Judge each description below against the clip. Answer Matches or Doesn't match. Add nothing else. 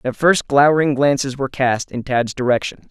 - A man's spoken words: Matches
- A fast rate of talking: Doesn't match